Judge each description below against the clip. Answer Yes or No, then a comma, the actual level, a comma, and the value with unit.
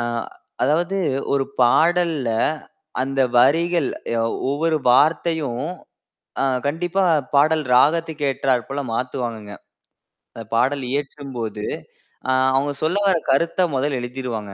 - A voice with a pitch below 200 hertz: Yes, medium, 140 Hz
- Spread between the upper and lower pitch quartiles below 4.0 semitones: No, average, 4.5 semitones